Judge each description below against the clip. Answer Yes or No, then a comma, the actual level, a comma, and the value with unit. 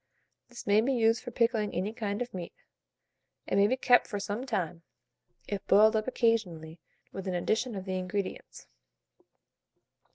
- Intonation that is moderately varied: Yes, average, 3.5 semitones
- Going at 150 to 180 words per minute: Yes, average, 160 wpm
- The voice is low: No, high, 210 Hz